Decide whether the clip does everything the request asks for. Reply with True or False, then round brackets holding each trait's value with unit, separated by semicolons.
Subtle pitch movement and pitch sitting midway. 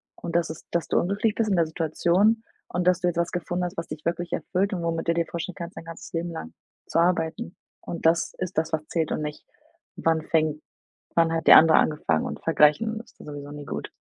True (1.9 semitones; 170 Hz)